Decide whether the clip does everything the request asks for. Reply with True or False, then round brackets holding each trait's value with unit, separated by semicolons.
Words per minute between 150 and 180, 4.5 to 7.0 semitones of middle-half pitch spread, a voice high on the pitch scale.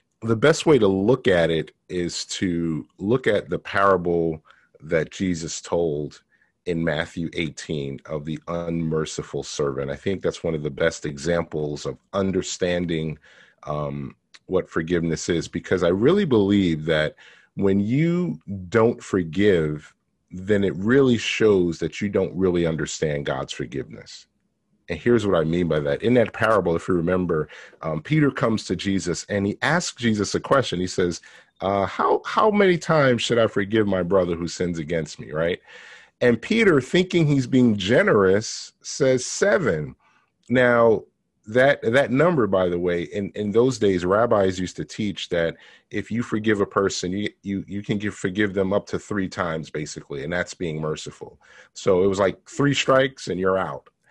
False (170 wpm; 5.2 semitones; 95 Hz)